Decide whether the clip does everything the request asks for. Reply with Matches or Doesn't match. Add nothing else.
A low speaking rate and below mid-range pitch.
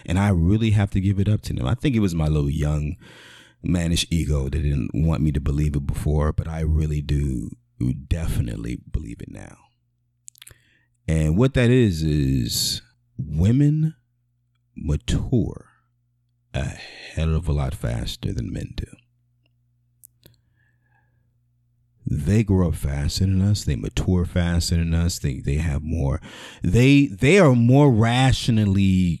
Doesn't match